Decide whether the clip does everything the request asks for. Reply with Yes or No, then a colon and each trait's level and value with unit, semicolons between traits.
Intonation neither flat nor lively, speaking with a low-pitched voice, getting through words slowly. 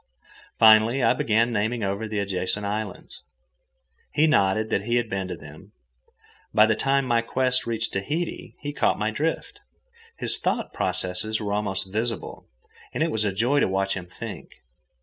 No: average, 3.5 semitones; low, 110 Hz; average, 170 wpm